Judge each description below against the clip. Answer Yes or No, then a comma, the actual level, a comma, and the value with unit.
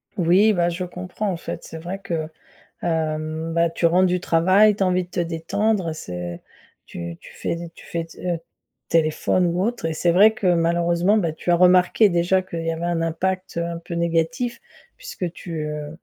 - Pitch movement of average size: No, narrow, 2.0 semitones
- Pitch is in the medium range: Yes, medium, 170 Hz